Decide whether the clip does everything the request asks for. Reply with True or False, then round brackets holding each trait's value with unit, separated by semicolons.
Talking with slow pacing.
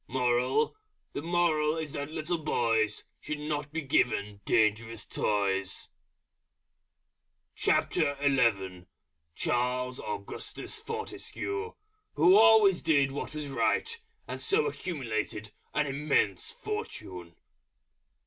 True (90 wpm)